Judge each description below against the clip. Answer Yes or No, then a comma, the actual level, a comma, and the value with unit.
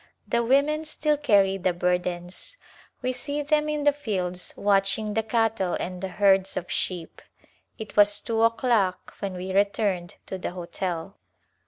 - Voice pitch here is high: Yes, high, 200 Hz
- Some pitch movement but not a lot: Yes, average, 4.4 semitones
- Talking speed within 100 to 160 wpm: Yes, average, 155 wpm